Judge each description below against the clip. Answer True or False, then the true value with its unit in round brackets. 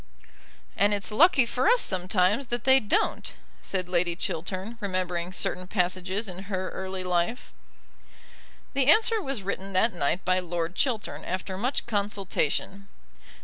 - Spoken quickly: False (145 wpm)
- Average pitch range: True (3.7 semitones)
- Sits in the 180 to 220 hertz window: True (190 Hz)